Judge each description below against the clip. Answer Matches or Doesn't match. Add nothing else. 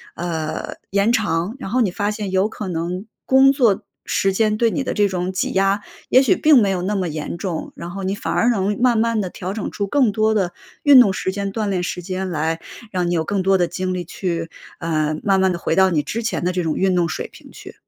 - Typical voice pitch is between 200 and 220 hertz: Doesn't match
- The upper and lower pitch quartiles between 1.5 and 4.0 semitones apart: Matches